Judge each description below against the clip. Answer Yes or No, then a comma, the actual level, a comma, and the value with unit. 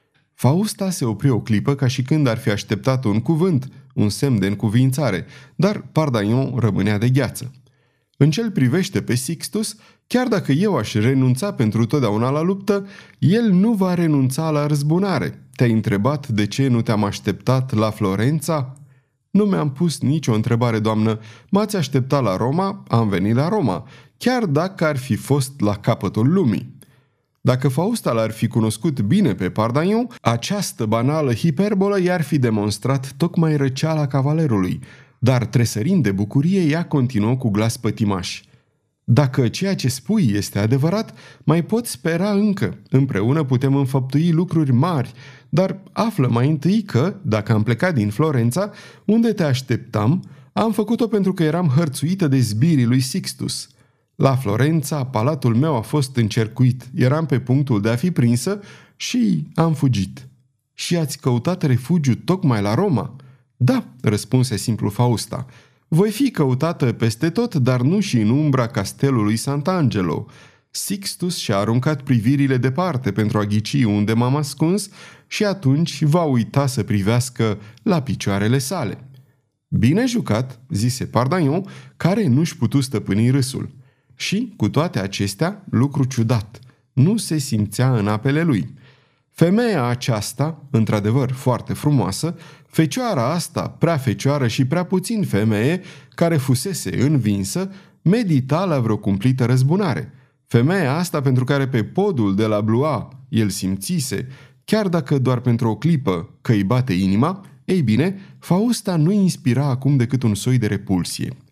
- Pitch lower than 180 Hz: Yes, low, 135 Hz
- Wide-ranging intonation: Yes, wide, 5.8 semitones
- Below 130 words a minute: No, average, 145 wpm